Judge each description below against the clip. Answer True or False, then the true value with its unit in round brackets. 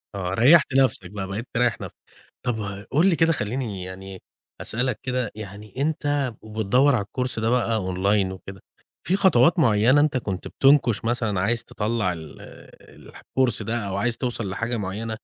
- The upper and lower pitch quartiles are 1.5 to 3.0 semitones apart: False (4.3 semitones)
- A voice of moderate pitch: False (115 Hz)